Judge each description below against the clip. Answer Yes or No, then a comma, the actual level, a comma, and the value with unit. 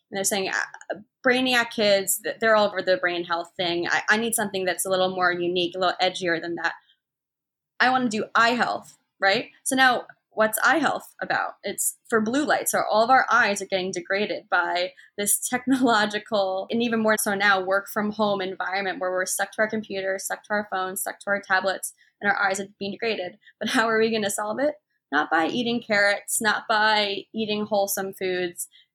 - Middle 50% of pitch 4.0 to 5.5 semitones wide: No, average, 2.8 semitones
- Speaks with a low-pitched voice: No, high, 200 Hz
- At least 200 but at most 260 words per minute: Yes, fast, 205 wpm